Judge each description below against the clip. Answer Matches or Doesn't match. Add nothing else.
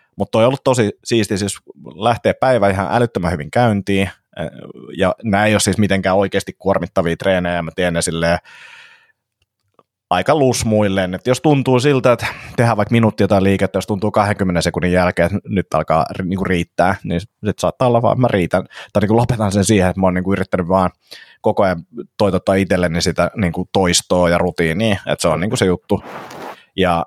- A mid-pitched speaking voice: Doesn't match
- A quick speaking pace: Matches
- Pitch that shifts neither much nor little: Matches